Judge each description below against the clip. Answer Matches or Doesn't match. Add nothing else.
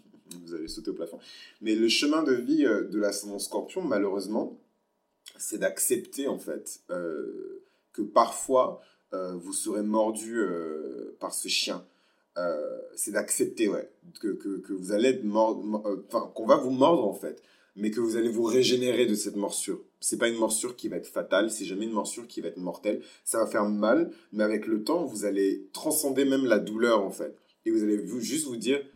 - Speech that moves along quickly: Doesn't match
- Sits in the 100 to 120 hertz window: Matches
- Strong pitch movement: Matches